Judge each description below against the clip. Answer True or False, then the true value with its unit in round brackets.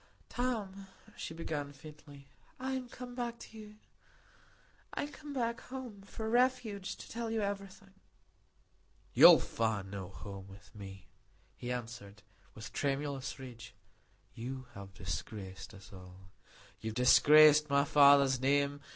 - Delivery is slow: True (130 wpm)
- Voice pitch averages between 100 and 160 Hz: True (140 Hz)